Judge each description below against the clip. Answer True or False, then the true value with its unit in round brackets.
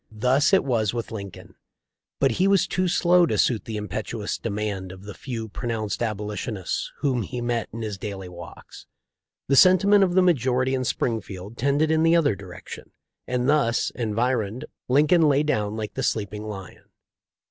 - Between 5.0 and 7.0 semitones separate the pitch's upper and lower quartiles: True (5.4 semitones)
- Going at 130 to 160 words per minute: False (180 wpm)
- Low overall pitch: True (120 Hz)